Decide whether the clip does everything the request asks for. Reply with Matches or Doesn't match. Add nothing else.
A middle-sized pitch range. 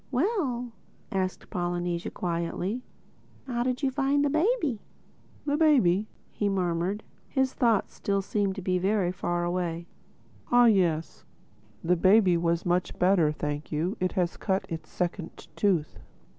Doesn't match